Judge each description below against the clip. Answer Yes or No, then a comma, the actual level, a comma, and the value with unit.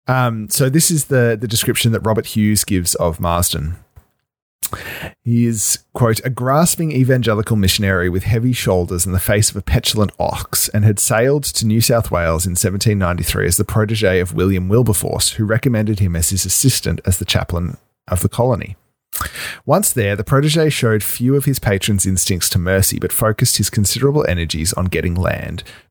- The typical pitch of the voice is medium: No, low, 110 Hz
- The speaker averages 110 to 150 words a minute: No, average, 180 wpm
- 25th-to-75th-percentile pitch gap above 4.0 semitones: Yes, average, 4.6 semitones